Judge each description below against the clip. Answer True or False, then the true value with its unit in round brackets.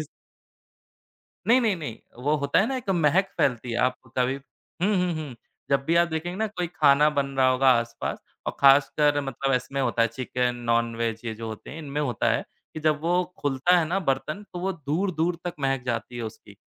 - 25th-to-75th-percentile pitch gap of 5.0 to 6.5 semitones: True (5.3 semitones)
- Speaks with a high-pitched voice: False (140 Hz)